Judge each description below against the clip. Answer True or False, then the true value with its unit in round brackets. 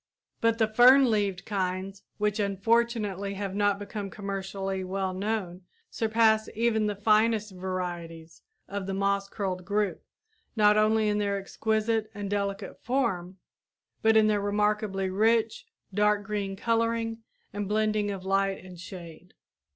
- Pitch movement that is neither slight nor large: False (2.1 semitones)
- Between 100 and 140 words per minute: True (135 wpm)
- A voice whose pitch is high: True (205 Hz)